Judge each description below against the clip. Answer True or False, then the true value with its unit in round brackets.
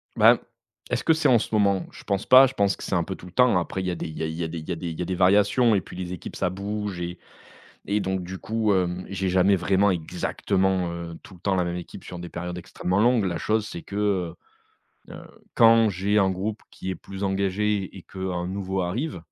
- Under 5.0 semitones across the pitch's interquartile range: True (2.5 semitones)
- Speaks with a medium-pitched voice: False (95 Hz)